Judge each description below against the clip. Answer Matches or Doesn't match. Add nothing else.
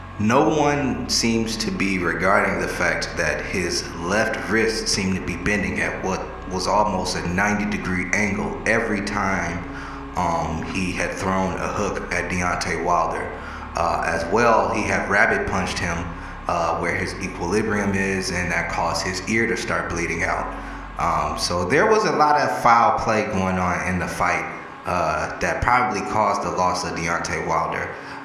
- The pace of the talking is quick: Doesn't match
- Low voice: Matches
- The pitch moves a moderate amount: Matches